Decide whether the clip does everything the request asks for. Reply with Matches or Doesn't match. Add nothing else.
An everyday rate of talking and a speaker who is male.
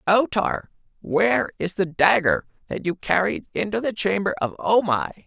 Matches